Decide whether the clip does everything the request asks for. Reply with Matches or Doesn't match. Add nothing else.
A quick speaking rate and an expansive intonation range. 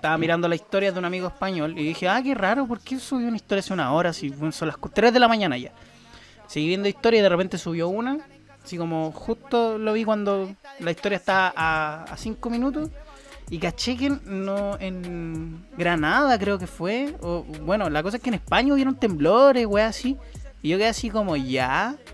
Matches